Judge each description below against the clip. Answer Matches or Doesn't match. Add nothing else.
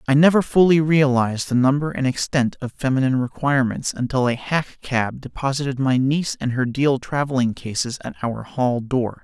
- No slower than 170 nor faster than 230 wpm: Matches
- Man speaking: Matches